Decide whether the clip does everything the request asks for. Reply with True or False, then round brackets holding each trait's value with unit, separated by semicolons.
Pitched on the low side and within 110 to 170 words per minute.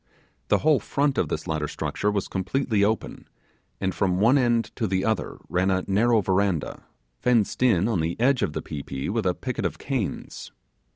False (100 Hz; 190 wpm)